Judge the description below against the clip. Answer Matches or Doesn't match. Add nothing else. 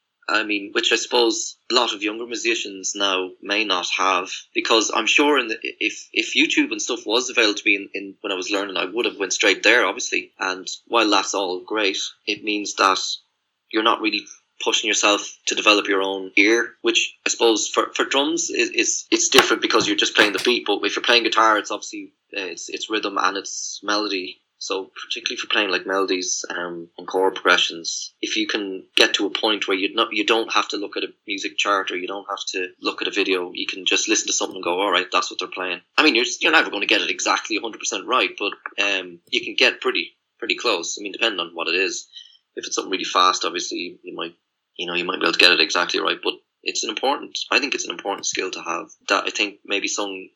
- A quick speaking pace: Matches